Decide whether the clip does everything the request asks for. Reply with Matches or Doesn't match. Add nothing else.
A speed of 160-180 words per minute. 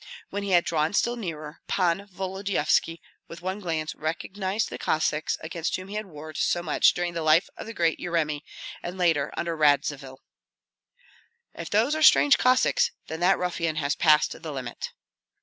Matches